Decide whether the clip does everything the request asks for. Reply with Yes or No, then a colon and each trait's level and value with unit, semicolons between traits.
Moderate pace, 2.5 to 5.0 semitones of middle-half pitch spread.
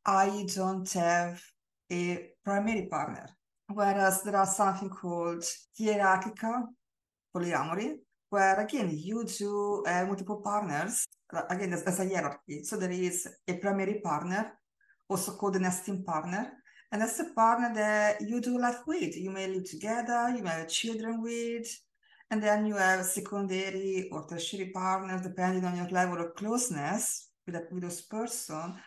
Yes: average, 150 wpm; average, 3.3 semitones